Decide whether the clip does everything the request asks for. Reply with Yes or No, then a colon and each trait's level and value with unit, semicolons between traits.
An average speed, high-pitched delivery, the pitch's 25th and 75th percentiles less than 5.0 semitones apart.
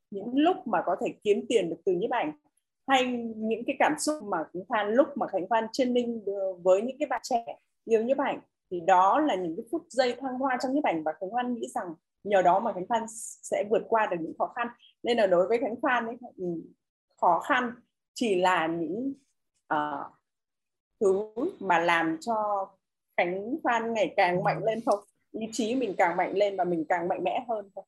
No: average, 215 wpm; high, 225 Hz; wide, 5.6 semitones